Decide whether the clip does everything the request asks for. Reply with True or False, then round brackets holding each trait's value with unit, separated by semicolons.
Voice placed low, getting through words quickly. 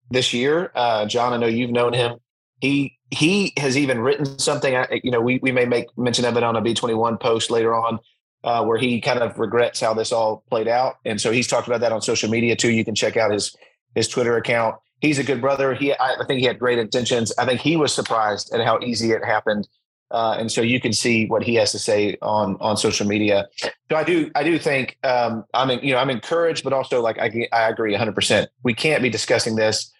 True (120 Hz; 250 wpm)